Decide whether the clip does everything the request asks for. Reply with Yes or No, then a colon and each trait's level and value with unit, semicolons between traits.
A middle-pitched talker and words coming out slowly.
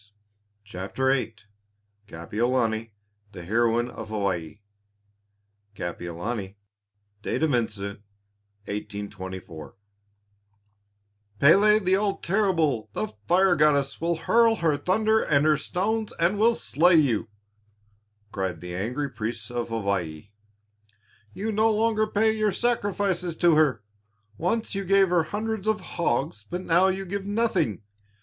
Yes: medium, 150 Hz; slow, 120 wpm